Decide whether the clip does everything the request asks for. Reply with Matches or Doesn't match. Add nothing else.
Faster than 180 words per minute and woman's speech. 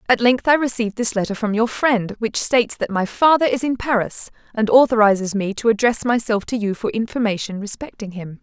Matches